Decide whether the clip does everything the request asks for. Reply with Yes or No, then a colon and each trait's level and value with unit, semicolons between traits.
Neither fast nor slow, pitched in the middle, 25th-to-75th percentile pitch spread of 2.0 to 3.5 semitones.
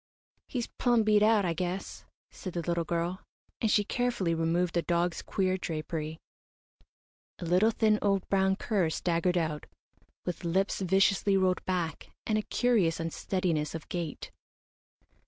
Yes: average, 145 wpm; medium, 180 Hz; average, 3.1 semitones